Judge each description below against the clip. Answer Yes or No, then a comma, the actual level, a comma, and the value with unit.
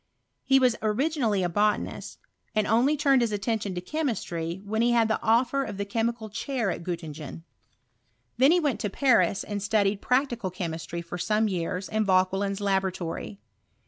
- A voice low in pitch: No, high, 210 Hz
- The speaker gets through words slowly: No, average, 175 wpm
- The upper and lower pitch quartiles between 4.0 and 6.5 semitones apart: Yes, average, 4.3 semitones